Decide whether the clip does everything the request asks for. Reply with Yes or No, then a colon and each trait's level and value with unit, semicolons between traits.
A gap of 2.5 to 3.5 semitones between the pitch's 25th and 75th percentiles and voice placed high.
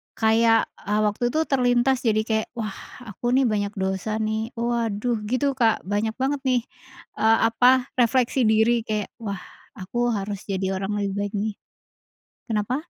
Yes: average, 2.8 semitones; high, 220 Hz